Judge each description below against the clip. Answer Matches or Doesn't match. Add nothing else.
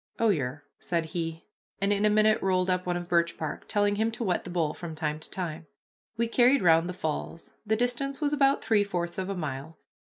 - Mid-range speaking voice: Matches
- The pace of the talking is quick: Matches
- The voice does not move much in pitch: Doesn't match